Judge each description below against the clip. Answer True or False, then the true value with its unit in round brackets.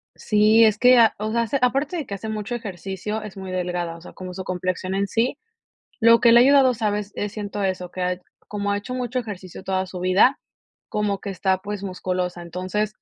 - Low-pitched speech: False (205 Hz)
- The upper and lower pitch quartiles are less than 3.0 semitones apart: False (3.3 semitones)